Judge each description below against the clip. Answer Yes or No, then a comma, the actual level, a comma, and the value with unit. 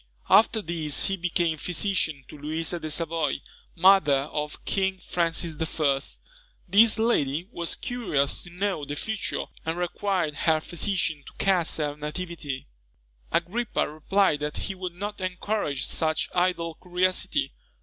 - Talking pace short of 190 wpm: Yes, slow, 135 wpm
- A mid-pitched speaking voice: Yes, medium, 170 Hz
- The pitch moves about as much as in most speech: Yes, average, 4.0 semitones